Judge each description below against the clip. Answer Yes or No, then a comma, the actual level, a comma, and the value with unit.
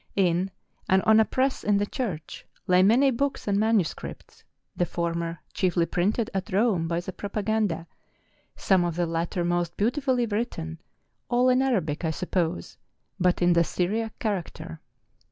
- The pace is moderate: Yes, average, 150 wpm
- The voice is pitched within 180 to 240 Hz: Yes, high, 190 Hz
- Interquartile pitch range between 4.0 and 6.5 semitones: Yes, average, 4.4 semitones